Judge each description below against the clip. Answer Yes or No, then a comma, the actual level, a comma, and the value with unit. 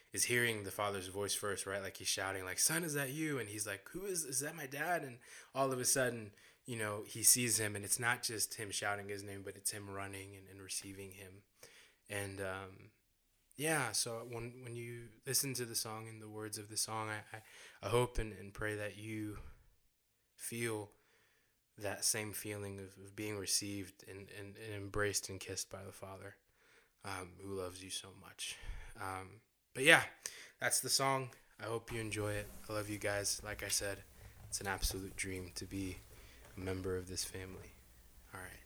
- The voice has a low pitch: Yes, low, 105 Hz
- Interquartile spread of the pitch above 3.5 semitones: No, average, 2.8 semitones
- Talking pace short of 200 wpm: No, fast, 205 wpm